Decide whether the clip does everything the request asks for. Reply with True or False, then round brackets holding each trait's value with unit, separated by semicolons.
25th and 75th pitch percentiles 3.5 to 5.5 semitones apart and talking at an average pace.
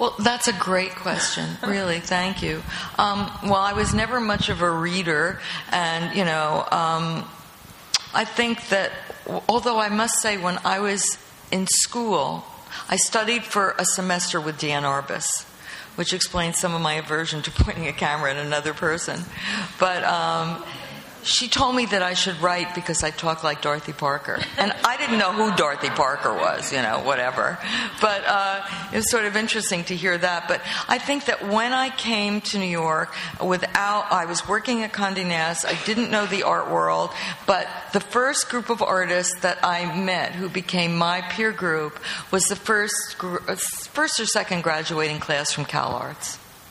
True (4.0 semitones; 175 wpm)